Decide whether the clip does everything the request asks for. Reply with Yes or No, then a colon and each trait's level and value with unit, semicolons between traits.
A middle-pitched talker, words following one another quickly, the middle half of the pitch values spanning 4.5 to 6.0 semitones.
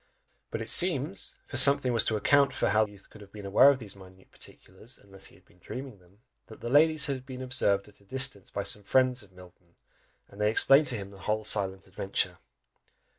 No: low, 105 Hz; fast, 225 wpm; average, 4.9 semitones